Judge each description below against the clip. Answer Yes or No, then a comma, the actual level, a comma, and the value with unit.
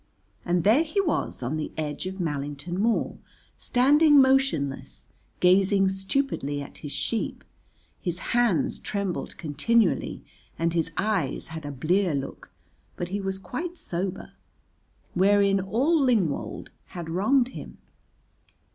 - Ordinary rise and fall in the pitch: No, wide, 6.3 semitones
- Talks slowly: Yes, slow, 125 wpm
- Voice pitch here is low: No, high, 190 Hz